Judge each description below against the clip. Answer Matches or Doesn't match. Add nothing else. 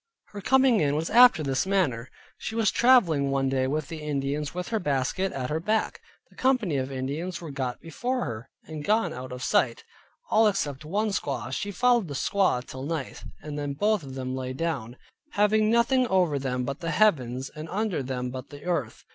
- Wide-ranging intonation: Matches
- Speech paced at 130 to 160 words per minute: Doesn't match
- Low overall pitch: Doesn't match